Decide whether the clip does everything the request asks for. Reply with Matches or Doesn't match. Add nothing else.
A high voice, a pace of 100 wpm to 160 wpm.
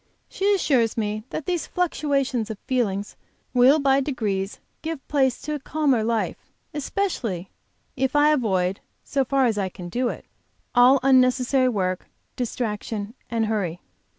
Matches